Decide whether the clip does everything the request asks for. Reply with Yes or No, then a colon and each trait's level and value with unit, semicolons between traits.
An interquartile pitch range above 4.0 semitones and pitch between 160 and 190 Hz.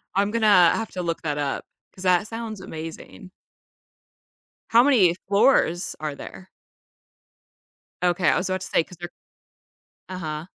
No: average, 3.4 semitones; medium, 185 Hz